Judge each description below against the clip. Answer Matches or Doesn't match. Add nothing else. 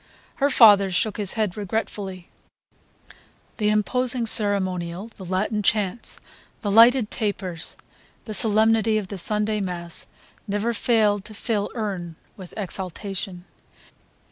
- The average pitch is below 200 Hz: Doesn't match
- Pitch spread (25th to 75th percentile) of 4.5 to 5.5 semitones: Doesn't match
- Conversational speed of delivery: Doesn't match